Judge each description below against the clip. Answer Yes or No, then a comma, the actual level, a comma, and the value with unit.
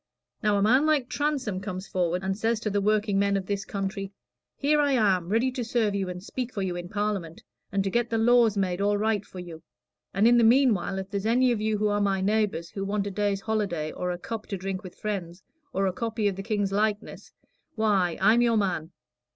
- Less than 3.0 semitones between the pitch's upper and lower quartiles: Yes, narrow, 2.6 semitones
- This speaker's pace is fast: Yes, fast, 230 wpm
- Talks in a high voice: Yes, high, 205 Hz